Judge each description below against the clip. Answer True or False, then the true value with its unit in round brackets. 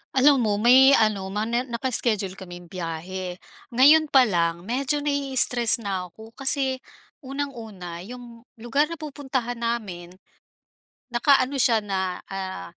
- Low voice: False (235 Hz)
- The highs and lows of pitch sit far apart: True (5.8 semitones)